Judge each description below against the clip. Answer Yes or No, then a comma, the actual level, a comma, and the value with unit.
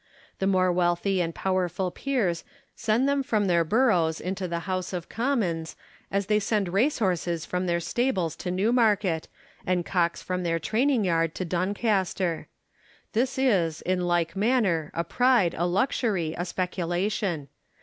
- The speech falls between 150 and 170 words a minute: Yes, average, 160 wpm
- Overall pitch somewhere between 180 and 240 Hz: Yes, medium, 185 Hz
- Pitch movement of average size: Yes, average, 3.8 semitones